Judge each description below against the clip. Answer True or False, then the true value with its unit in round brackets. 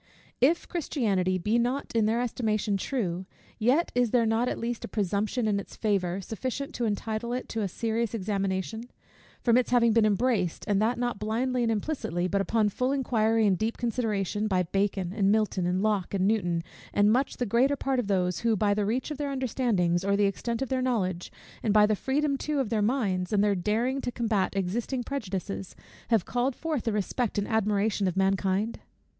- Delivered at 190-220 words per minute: True (200 wpm)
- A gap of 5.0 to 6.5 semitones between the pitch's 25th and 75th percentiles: False (3.7 semitones)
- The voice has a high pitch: True (220 Hz)